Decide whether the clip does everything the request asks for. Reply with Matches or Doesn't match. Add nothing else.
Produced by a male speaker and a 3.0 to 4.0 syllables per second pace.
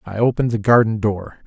Doesn't match